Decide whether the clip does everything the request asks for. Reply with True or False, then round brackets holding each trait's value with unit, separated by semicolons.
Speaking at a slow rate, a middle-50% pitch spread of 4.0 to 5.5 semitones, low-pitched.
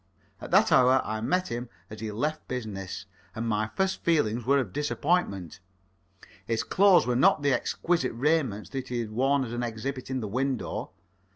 False (180 wpm; 4.3 semitones; 125 Hz)